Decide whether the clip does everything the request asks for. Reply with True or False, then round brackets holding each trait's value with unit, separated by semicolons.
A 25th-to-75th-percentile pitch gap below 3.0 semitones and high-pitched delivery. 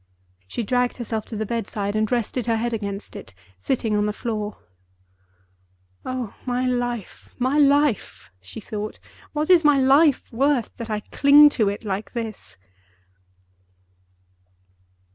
False (3.7 semitones; 235 Hz)